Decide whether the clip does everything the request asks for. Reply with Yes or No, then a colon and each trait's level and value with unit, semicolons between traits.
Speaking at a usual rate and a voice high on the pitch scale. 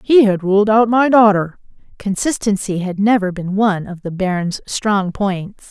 Yes: average, 170 wpm; high, 200 Hz